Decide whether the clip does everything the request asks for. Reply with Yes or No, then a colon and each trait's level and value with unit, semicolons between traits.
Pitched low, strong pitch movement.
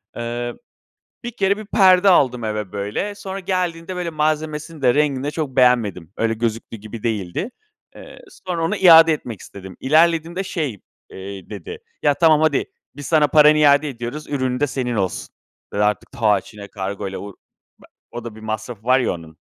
Yes: low, 130 Hz; wide, 6.9 semitones